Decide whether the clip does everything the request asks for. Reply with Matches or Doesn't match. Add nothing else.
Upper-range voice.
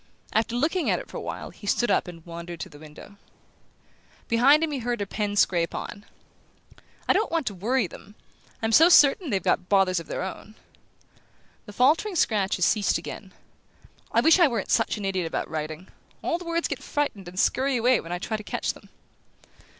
Matches